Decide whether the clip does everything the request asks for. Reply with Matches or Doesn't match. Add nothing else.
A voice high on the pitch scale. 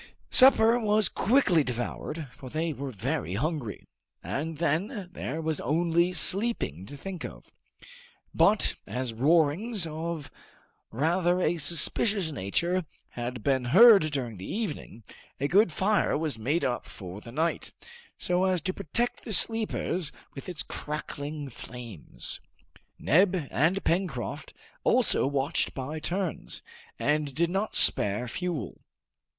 Doesn't match